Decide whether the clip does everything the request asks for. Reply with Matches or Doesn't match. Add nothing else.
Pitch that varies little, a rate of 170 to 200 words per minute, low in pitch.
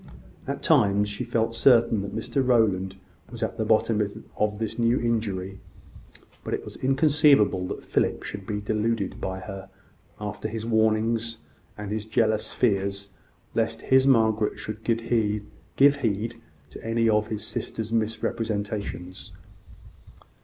Doesn't match